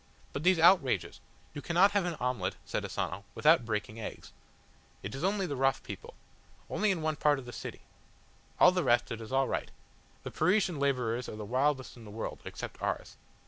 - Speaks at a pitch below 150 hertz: Yes, low, 135 Hz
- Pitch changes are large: Yes, wide, 6.7 semitones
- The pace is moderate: Yes, average, 190 wpm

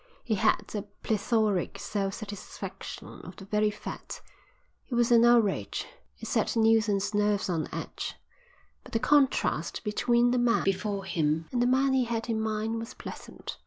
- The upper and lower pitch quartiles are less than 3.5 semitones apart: Yes, average, 3.0 semitones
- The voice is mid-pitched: No, high, 220 Hz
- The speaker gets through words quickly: No, average, 165 wpm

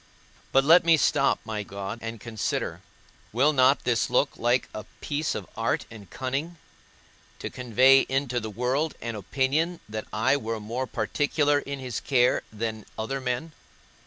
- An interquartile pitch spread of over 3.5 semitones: Yes, average, 4.0 semitones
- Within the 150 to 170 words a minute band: Yes, average, 160 wpm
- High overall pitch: No, low, 125 Hz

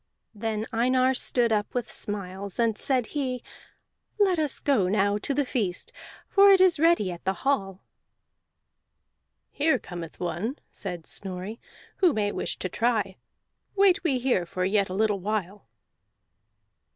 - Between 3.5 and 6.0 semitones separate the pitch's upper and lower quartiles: Yes, wide, 5.6 semitones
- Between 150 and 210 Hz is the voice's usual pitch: No, high, 220 Hz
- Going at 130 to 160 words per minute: Yes, average, 145 wpm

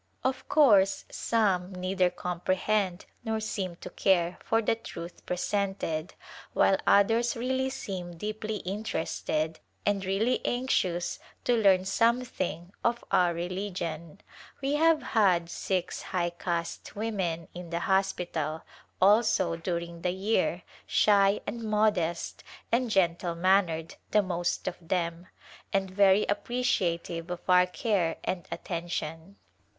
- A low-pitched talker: No, high, 190 Hz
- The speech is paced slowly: Yes, slow, 125 wpm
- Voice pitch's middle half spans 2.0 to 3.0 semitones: No, average, 3.7 semitones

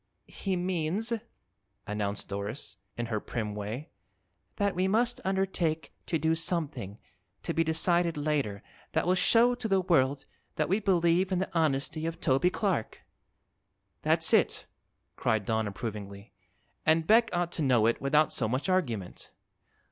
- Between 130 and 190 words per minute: Yes, average, 150 wpm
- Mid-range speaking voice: Yes, medium, 160 Hz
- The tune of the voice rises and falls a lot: Yes, wide, 7.9 semitones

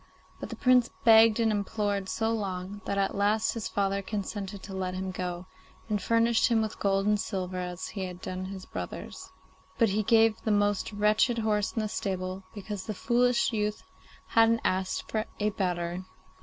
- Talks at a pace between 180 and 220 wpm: Yes, average, 185 wpm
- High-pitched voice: Yes, high, 205 Hz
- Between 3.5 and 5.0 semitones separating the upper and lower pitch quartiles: No, average, 2.7 semitones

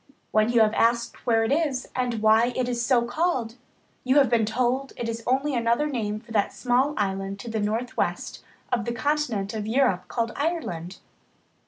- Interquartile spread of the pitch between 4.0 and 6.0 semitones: No, average, 2.8 semitones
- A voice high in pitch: Yes, high, 235 Hz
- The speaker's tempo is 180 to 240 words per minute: Yes, average, 185 wpm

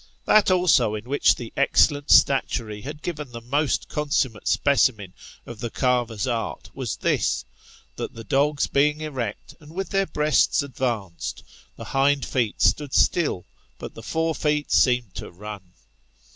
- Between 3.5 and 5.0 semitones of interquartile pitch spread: Yes, average, 4.6 semitones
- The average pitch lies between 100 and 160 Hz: Yes, low, 135 Hz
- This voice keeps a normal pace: Yes, average, 155 wpm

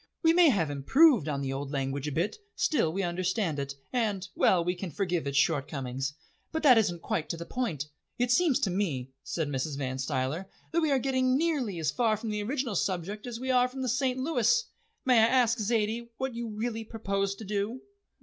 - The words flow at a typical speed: No, fast, 210 wpm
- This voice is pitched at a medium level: No, high, 205 Hz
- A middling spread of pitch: No, wide, 8.0 semitones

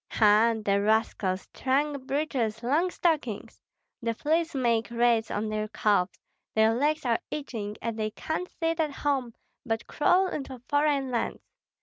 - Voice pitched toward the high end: Yes, high, 240 Hz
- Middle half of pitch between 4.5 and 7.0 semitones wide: Yes, average, 5.1 semitones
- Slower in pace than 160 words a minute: Yes, average, 145 wpm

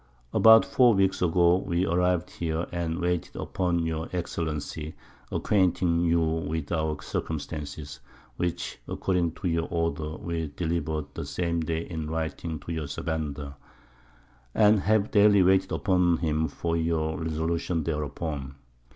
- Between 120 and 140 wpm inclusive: Yes, slow, 135 wpm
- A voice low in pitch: Yes, very low, 85 Hz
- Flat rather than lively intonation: Yes, narrow, 2.0 semitones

